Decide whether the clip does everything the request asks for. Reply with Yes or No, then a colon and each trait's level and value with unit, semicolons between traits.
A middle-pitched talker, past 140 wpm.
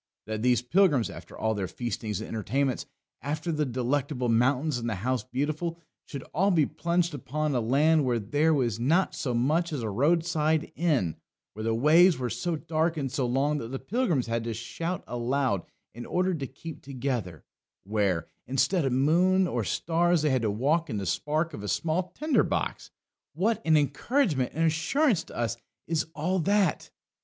Yes: medium, 145 Hz; average, 185 wpm